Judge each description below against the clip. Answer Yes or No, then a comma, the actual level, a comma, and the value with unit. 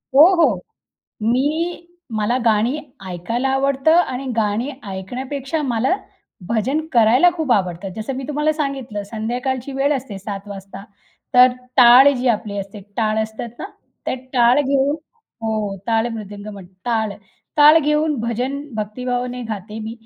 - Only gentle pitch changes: No, average, 4.4 semitones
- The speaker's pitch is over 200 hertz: Yes, high, 240 Hz